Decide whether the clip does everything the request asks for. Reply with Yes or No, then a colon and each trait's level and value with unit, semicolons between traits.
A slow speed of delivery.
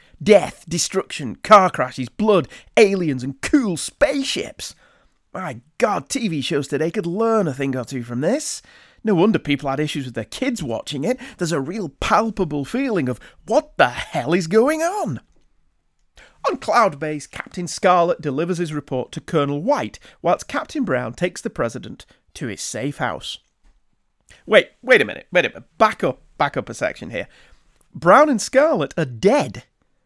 No: average, 170 wpm